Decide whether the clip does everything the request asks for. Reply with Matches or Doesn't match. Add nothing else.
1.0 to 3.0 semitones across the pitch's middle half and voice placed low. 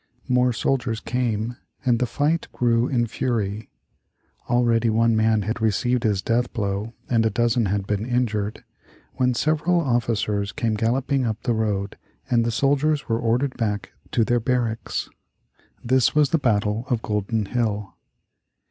Matches